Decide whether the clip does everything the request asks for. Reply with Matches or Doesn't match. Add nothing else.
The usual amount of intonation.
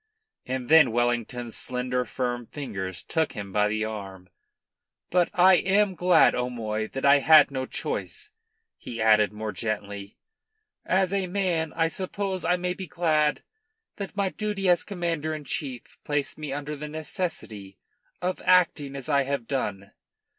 Doesn't match